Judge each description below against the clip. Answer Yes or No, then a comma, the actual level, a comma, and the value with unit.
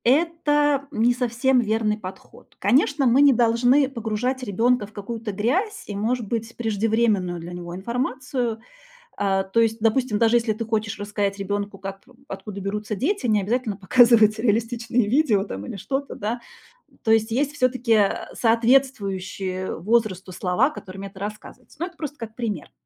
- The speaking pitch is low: No, high, 225 Hz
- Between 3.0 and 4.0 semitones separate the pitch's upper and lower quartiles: Yes, average, 3.7 semitones